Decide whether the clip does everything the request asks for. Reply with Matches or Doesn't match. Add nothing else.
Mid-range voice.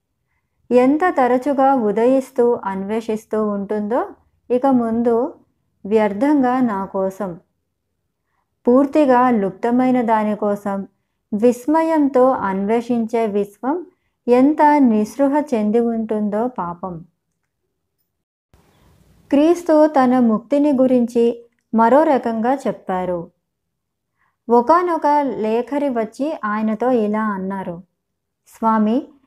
Doesn't match